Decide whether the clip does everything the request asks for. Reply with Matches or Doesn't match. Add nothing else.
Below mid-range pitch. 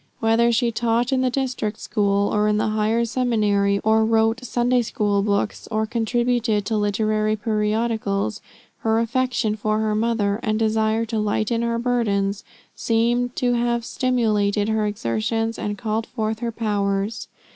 Doesn't match